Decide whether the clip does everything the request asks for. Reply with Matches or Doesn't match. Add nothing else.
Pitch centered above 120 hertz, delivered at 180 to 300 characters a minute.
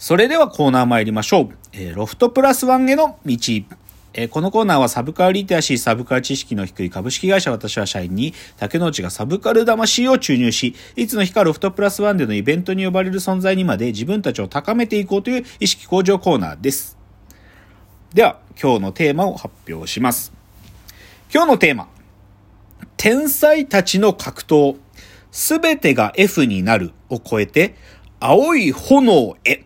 Doesn't match